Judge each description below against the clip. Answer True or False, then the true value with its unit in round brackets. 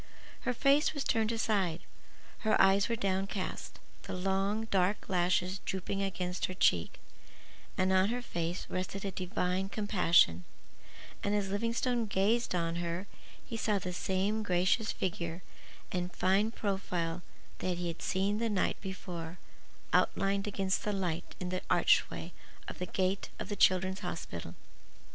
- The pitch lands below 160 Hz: False (190 Hz)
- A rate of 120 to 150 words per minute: True (145 wpm)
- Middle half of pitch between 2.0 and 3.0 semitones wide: True (2.4 semitones)